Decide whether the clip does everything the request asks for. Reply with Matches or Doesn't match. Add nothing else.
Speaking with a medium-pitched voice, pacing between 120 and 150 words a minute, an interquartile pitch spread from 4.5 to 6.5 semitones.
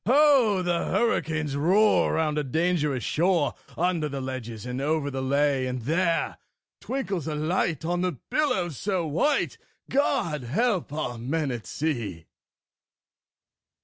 Matches